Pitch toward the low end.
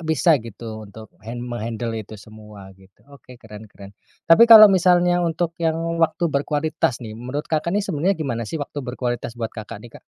Yes: low, 125 Hz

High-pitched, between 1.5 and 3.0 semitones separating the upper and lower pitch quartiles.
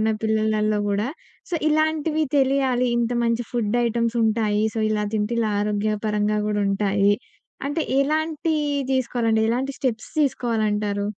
No: high, 225 Hz; average, 3.6 semitones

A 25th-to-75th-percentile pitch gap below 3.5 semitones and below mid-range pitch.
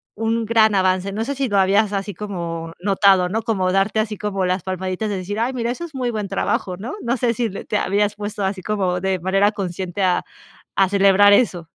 No: narrow, 2.6 semitones; high, 200 Hz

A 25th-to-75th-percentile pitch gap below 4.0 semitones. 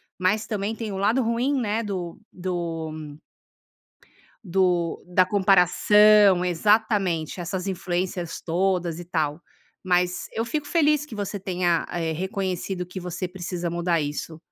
Yes: average, 3.0 semitones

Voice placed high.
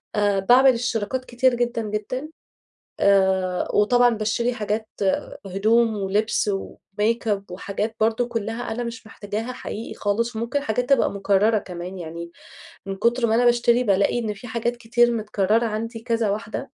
Yes: high, 220 Hz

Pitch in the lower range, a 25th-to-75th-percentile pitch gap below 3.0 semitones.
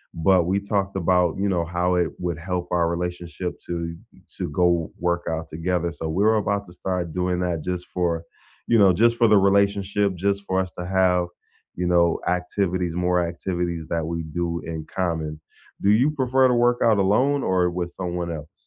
Yes: very low, 90 Hz; narrow, 2.4 semitones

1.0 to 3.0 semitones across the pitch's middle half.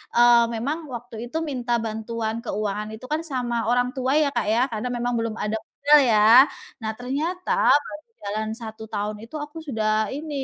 No: average, 3.5 semitones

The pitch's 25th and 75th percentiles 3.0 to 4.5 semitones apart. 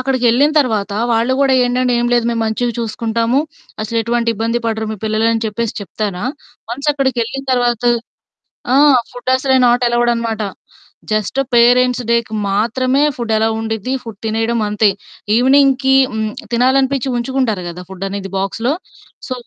No: narrow, 2.5 semitones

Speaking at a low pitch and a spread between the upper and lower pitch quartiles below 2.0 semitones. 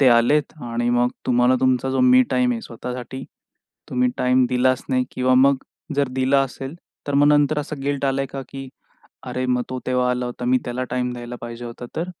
Yes: low, 125 Hz; narrow, 1.5 semitones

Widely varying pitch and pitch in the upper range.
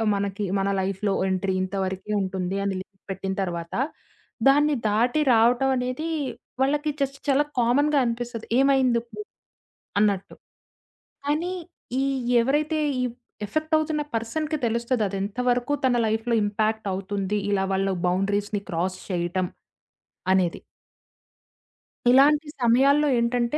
Yes: wide, 5.8 semitones; high, 230 Hz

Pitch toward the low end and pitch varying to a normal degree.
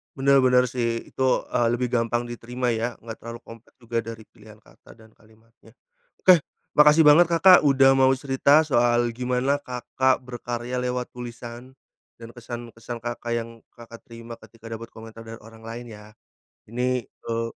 No: low, 120 Hz; narrow, 1.8 semitones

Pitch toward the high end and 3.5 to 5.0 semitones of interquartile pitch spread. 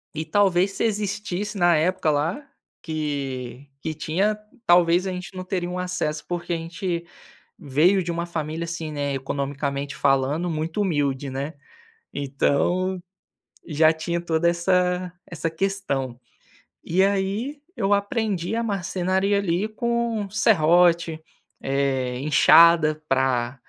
No: medium, 170 Hz; average, 4.2 semitones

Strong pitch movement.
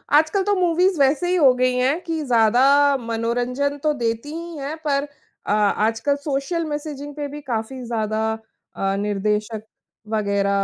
No: average, 4.9 semitones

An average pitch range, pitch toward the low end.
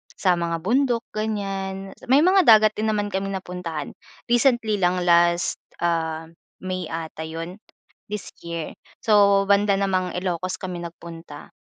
No: average, 3.4 semitones; medium, 185 Hz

